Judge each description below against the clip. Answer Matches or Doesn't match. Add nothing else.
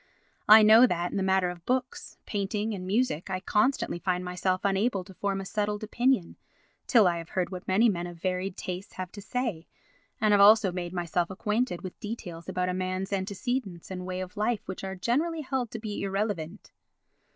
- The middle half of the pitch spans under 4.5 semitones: Matches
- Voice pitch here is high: Matches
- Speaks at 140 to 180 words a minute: Doesn't match